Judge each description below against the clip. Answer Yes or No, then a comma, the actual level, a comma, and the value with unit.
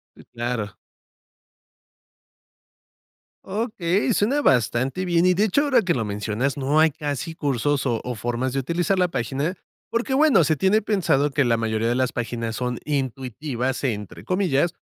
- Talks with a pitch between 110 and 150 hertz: Yes, medium, 140 Hz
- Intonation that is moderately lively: No, wide, 7.1 semitones